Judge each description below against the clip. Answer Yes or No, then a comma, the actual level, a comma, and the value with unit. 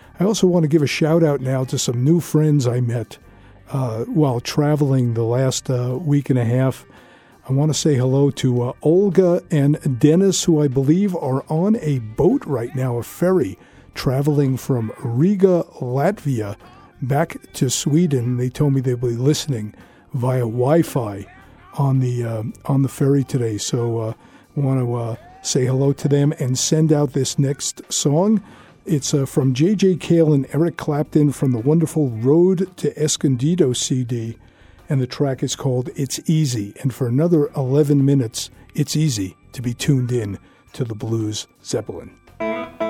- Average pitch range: Yes, average, 3.7 semitones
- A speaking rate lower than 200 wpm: Yes, average, 170 wpm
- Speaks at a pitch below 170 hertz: Yes, medium, 140 Hz